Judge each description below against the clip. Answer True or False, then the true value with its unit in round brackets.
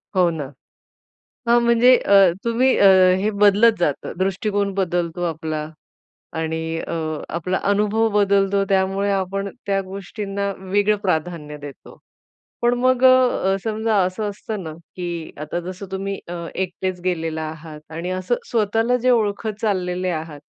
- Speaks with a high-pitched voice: True (195 Hz)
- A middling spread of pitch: True (3.4 semitones)